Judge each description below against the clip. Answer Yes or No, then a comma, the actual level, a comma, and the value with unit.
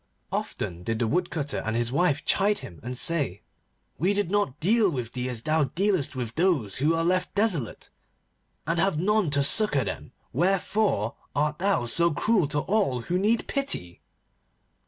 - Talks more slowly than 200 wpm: Yes, average, 170 wpm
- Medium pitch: Yes, medium, 155 Hz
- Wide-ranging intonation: Yes, wide, 7.5 semitones